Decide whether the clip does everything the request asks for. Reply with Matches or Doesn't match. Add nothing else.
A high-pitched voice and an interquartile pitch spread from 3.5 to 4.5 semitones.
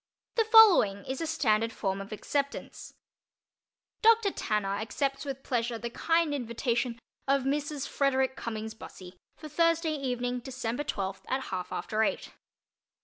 Doesn't match